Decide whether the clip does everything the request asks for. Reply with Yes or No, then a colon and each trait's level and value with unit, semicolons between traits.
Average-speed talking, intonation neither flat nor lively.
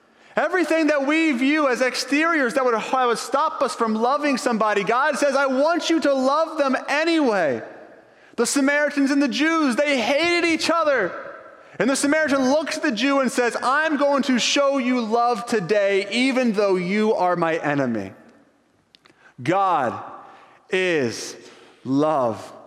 Yes: average, 150 wpm; average, 4.2 semitones